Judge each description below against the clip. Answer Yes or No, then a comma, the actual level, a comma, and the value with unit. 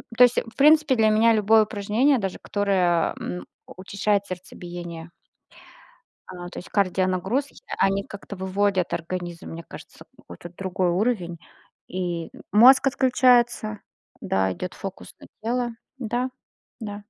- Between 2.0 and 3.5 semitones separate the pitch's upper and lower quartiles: No, average, 4.4 semitones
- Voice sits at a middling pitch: No, high, 200 Hz